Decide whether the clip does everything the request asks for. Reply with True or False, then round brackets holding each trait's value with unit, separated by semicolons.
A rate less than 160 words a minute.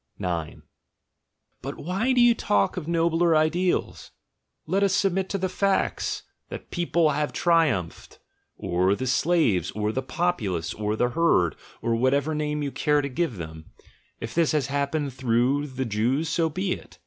False (170 wpm)